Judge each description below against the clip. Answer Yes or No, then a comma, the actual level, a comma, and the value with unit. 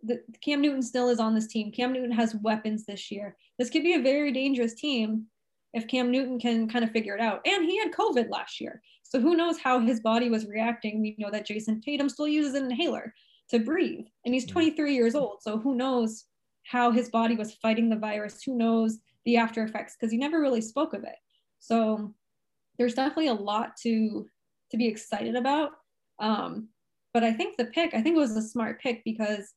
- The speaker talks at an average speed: No, fast, 215 wpm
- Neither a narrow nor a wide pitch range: Yes, average, 3.4 semitones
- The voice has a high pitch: Yes, high, 235 Hz